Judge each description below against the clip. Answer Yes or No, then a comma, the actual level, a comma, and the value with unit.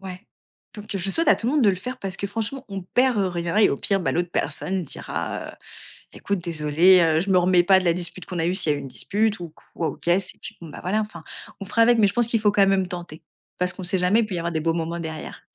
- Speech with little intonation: No, average, 3.2 semitones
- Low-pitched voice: No, medium, 185 Hz